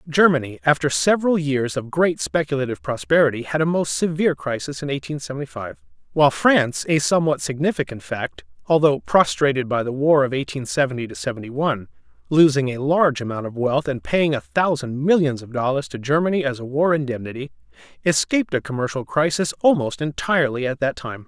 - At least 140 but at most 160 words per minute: No, average, 175 wpm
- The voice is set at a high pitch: No, medium, 140 Hz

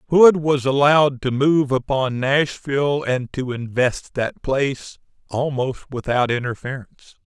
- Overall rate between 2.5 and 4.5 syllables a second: Yes, 4.3 syllables/s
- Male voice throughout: Yes, male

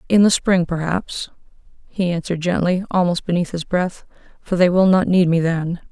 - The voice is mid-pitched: Yes, medium, 175 Hz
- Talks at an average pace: Yes, average, 170 wpm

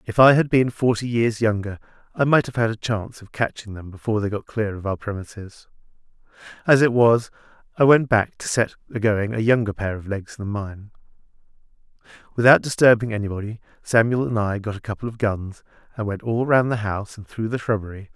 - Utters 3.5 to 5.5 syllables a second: No, 5.8 syllables/s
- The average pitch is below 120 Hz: Yes, low, 110 Hz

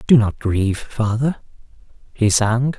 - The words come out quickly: No, slow, 130 wpm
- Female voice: No, male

